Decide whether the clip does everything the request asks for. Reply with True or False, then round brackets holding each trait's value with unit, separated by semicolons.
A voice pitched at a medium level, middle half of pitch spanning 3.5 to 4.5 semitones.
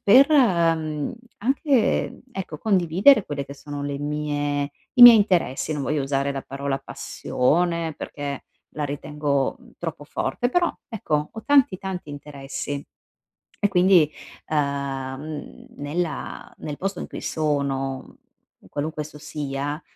True (150 Hz; 4.2 semitones)